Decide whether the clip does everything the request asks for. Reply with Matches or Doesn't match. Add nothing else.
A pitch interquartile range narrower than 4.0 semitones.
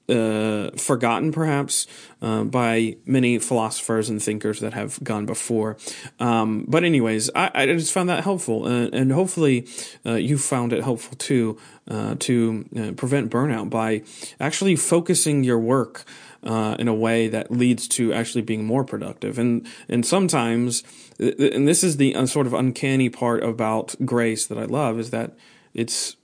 Matches